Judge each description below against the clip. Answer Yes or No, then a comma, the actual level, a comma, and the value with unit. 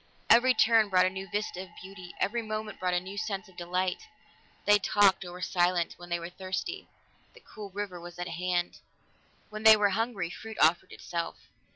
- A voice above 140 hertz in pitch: Yes, high, 190 Hz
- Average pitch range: Yes, average, 3.2 semitones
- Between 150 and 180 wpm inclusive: No, average, 195 wpm